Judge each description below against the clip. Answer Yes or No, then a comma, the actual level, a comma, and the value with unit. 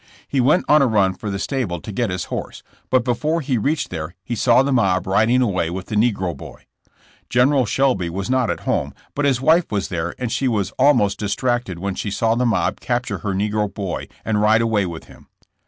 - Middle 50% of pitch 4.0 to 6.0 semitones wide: Yes, average, 4.7 semitones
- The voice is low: Yes, low, 110 Hz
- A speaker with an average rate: No, fast, 220 wpm